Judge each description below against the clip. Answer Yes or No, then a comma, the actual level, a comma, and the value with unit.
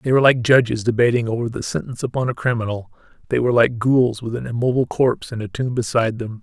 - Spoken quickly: Yes, fast, 225 wpm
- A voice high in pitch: No, low, 120 Hz